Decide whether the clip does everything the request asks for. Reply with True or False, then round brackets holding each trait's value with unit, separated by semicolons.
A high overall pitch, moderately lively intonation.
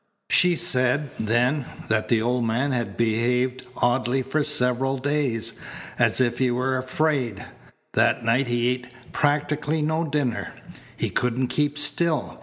False (130 Hz; 3.3 semitones)